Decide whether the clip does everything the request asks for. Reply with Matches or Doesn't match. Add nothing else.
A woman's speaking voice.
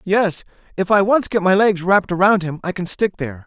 Doesn't match